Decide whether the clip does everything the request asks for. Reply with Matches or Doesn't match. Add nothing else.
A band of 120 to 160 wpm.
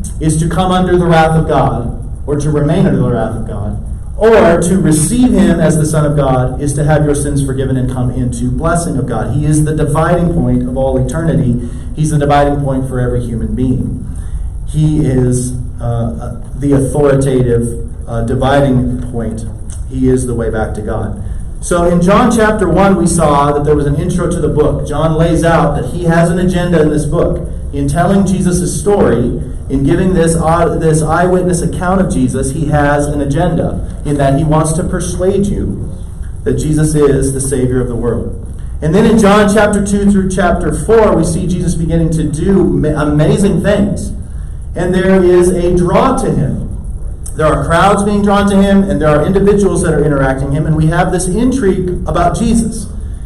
Doesn't match